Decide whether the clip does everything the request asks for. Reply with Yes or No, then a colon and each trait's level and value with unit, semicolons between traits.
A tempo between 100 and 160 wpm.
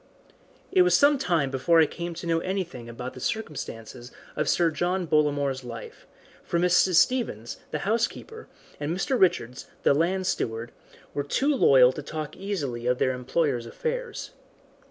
Yes: average, 155 wpm